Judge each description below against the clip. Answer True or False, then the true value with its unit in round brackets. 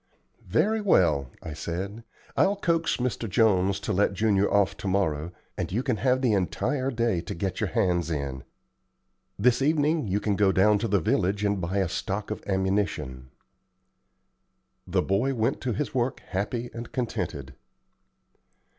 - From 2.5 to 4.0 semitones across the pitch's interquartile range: False (4.6 semitones)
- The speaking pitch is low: True (100 Hz)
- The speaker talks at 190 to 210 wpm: False (160 wpm)